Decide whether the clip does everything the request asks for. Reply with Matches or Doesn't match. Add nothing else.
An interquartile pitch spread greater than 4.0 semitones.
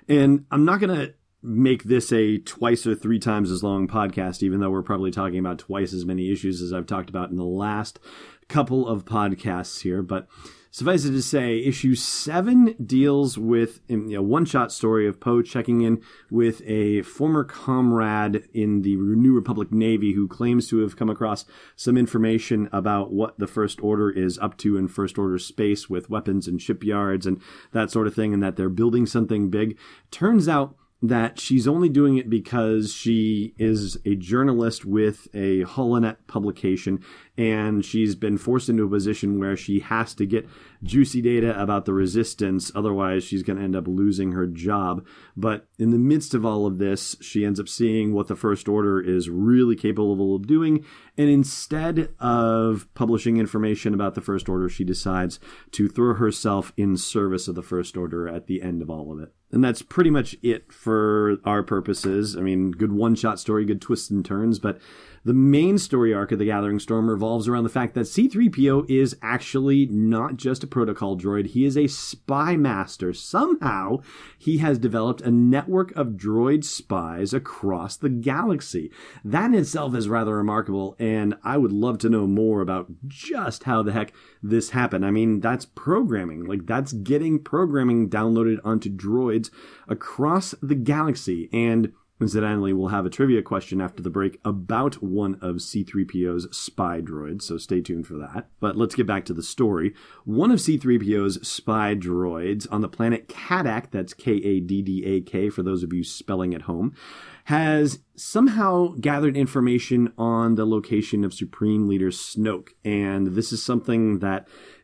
Doesn't match